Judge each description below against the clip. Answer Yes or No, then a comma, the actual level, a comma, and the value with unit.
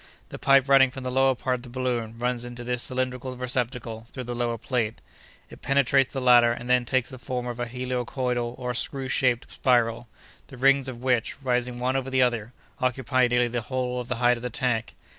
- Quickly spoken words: Yes, fast, 215 wpm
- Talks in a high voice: No, low, 125 Hz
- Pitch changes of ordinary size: No, narrow, 1.2 semitones